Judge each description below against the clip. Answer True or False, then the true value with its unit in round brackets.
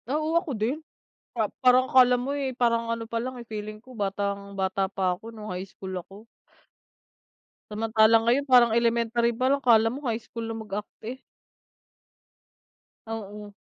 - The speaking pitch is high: True (230 Hz)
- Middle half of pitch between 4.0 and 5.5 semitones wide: False (3.1 semitones)